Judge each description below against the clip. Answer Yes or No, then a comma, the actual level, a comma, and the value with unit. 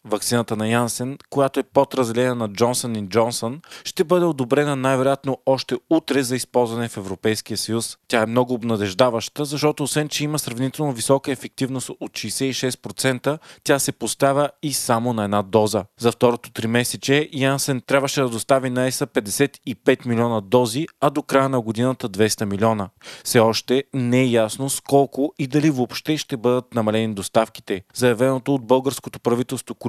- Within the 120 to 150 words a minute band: No, average, 160 wpm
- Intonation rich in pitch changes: No, average, 3.0 semitones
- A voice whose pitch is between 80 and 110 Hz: No, low, 130 Hz